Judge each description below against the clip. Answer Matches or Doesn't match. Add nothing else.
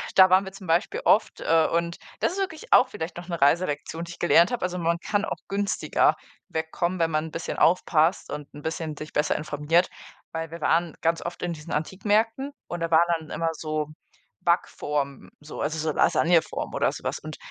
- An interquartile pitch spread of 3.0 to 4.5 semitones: Doesn't match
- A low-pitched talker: Doesn't match